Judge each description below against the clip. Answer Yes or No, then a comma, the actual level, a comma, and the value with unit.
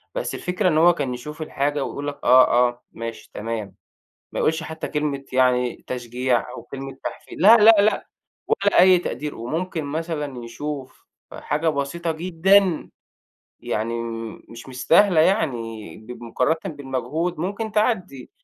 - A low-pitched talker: No, medium, 145 Hz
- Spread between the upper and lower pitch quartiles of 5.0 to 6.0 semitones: Yes, wide, 5.6 semitones